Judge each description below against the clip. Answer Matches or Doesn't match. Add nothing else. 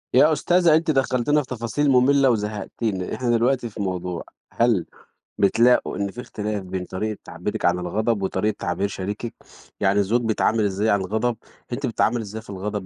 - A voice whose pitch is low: Matches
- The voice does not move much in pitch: Doesn't match